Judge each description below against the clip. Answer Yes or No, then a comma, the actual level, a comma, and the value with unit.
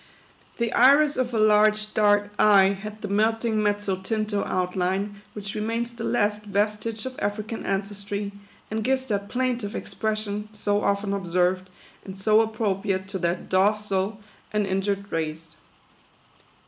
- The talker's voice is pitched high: Yes, high, 205 Hz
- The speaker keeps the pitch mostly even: Yes, narrow, 1.7 semitones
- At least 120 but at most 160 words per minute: Yes, average, 140 wpm